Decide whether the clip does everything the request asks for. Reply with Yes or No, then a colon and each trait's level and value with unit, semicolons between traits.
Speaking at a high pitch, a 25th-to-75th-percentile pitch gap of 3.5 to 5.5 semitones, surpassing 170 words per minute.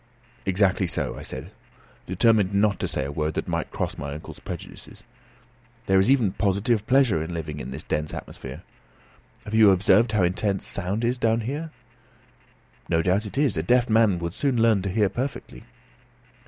No: low, 100 Hz; average, 4.3 semitones; average, 180 wpm